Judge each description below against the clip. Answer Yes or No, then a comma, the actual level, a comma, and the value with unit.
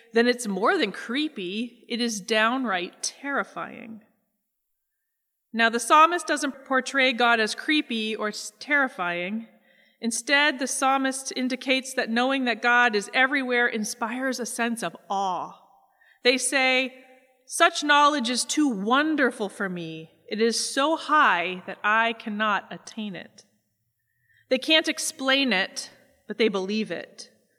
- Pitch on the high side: Yes, high, 240 Hz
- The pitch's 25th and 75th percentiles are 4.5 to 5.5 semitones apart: No, average, 3.7 semitones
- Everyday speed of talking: No, slow, 130 wpm